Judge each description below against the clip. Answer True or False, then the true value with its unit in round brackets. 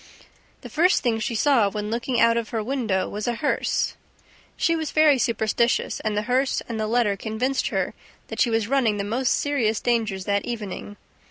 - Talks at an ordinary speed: True (190 wpm)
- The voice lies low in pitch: False (230 Hz)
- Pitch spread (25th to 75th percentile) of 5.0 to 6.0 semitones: False (3.2 semitones)